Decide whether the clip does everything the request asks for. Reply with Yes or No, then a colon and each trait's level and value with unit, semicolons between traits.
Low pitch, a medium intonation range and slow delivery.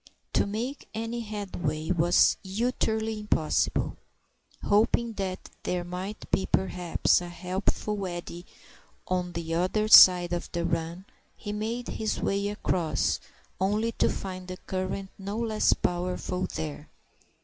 No: medium, 185 Hz; average, 3.3 semitones; slow, 125 wpm